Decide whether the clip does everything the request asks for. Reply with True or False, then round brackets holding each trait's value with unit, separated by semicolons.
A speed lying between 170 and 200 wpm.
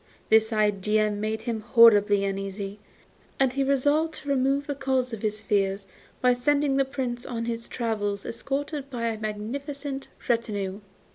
False (150 wpm)